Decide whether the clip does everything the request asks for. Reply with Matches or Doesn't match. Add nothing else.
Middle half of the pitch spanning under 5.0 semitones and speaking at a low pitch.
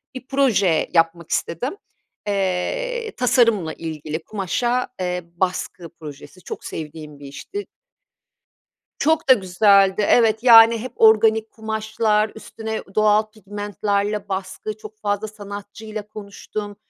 Doesn't match